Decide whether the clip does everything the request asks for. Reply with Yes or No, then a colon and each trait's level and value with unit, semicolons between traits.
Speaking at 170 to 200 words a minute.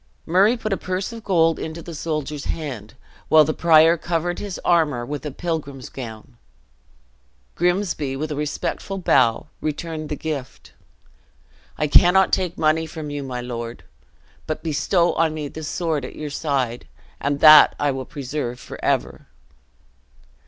No: average, 150 wpm